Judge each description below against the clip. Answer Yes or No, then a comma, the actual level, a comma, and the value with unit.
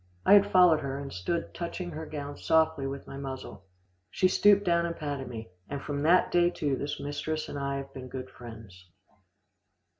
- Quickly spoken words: No, average, 190 wpm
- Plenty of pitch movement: No, average, 3.8 semitones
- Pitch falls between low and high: Yes, medium, 145 Hz